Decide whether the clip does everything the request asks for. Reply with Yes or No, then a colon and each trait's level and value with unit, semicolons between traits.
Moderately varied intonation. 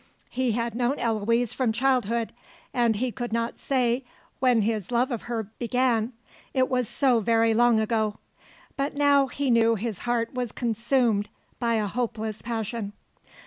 No: narrow, 2.0 semitones